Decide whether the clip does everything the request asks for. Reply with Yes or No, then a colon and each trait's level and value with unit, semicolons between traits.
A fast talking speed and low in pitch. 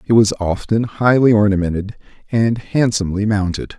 No: slow, 125 wpm; low, 105 Hz